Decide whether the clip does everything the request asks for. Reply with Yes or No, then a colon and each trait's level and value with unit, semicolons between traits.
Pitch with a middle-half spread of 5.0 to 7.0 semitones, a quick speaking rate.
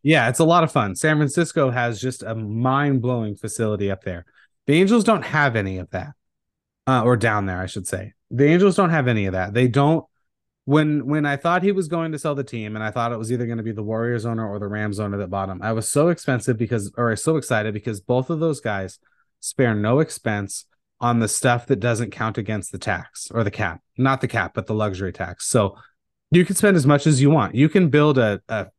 Yes: wide, 5.5 semitones; fast, 250 wpm